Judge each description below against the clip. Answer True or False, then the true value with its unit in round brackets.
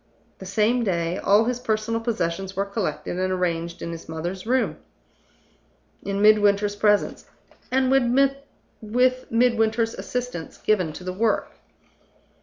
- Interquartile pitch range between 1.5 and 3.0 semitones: False (3.8 semitones)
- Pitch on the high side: True (205 Hz)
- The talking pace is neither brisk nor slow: False (125 wpm)